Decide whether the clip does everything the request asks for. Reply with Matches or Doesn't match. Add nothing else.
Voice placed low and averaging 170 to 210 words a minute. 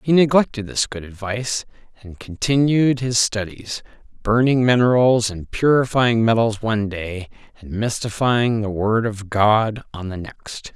Doesn't match